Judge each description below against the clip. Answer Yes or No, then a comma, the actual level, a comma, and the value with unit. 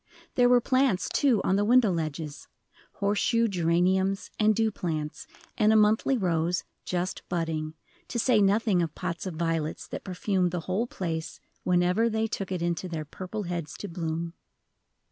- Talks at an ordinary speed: Yes, average, 165 wpm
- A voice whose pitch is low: No, medium, 185 Hz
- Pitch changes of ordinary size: Yes, average, 4.3 semitones